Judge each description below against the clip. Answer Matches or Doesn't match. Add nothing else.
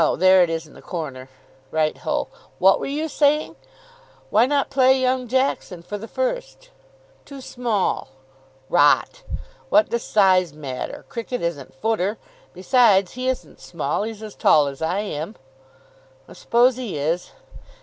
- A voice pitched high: Matches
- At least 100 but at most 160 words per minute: Matches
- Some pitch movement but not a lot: Doesn't match